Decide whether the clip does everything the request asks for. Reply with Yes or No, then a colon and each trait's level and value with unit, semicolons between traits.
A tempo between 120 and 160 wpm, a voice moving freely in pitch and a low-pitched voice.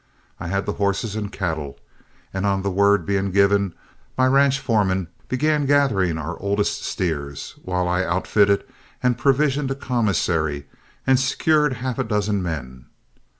Yes: average, 150 wpm; wide, 5.9 semitones; low, 100 Hz